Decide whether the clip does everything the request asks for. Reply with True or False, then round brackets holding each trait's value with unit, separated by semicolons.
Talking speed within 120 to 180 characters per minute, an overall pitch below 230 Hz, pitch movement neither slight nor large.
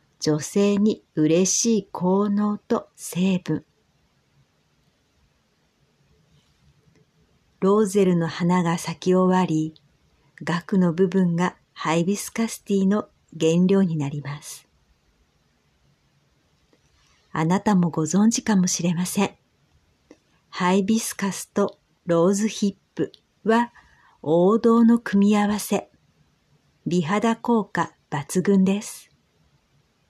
True (175 characters per minute; 185 Hz; 3.8 semitones)